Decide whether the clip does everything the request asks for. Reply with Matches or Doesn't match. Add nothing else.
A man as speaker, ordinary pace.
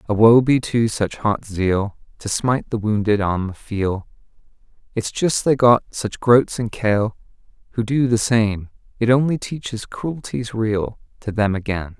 Matches